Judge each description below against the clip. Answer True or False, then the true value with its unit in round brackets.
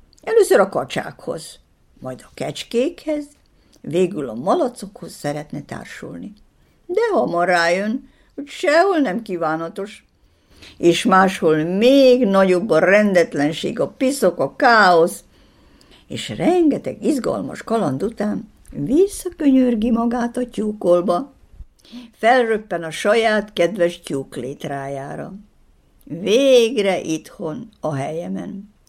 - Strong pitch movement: True (6.7 semitones)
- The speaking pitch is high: True (210 Hz)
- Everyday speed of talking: False (100 wpm)